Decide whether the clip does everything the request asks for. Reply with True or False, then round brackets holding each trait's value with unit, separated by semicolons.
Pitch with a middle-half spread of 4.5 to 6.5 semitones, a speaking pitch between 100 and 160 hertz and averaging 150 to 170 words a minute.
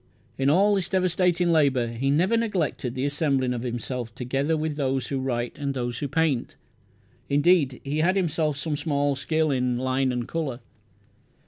False (3.9 semitones; 140 Hz; 165 wpm)